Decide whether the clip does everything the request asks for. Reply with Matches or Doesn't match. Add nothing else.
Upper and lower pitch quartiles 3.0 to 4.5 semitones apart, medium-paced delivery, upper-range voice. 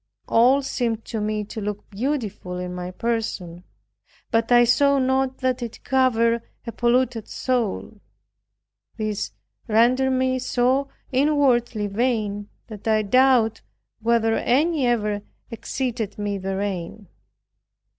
Doesn't match